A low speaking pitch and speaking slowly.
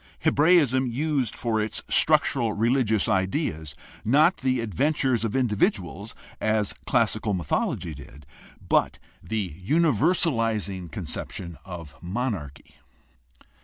Yes: low, 110 Hz; slow, 100 wpm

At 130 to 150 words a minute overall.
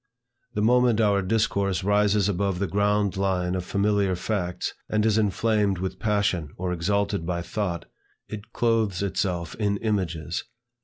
Yes: average, 145 wpm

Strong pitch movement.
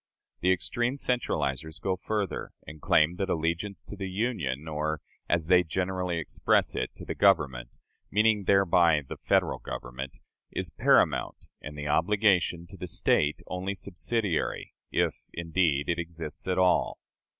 No: average, 3.9 semitones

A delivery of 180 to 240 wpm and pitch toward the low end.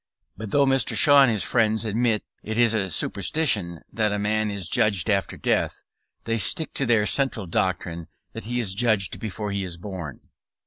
Yes: average, 185 wpm; low, 105 Hz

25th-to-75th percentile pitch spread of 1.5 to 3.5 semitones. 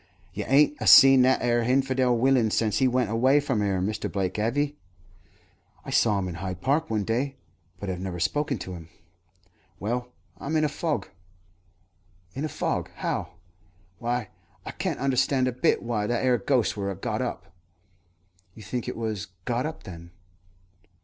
No: average, 4.6 semitones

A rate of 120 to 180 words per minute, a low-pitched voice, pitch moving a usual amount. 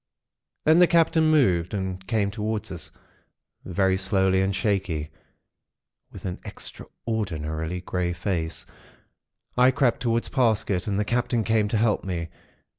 Yes: slow, 135 wpm; low, 100 Hz; average, 4.3 semitones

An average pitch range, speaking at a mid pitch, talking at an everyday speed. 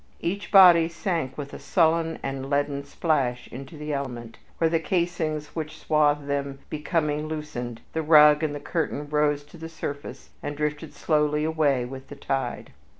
No: narrow, 2.3 semitones; medium, 150 Hz; average, 165 wpm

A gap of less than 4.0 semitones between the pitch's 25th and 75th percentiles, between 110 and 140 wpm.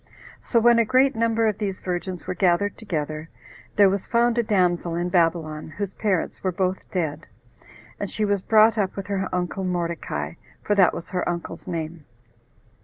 No: average, 3.5 semitones; average, 180 wpm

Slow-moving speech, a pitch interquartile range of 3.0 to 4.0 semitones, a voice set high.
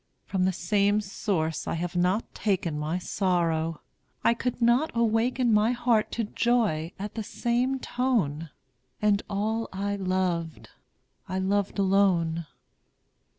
No: slow, 130 wpm; average, 4.5 semitones; high, 200 Hz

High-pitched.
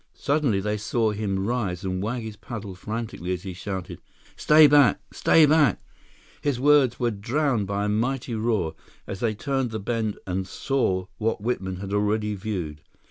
No: low, 110 Hz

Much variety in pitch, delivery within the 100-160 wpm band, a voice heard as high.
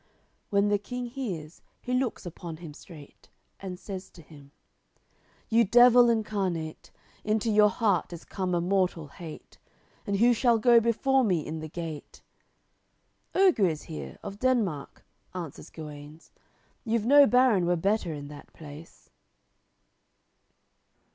Yes: wide, 6.4 semitones; slow, 135 wpm; high, 195 Hz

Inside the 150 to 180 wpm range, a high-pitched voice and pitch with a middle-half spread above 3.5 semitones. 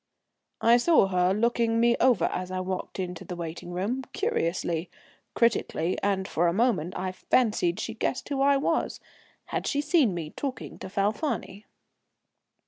Yes: average, 155 wpm; high, 200 Hz; average, 5.1 semitones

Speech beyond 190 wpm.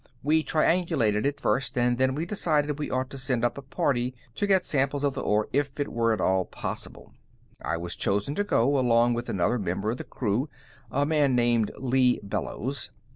Yes: average, 200 wpm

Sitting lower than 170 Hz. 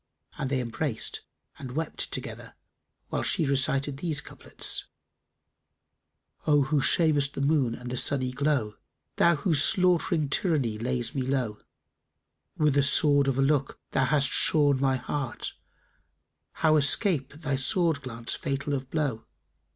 Yes: medium, 140 Hz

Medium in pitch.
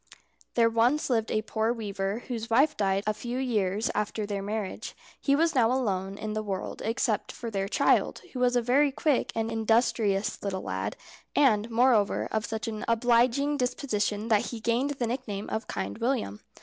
No: high, 225 Hz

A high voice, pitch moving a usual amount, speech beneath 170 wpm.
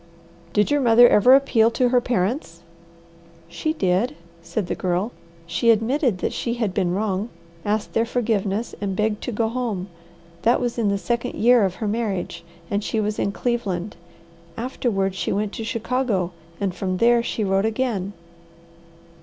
Yes: high, 215 Hz; average, 3.6 semitones; average, 160 wpm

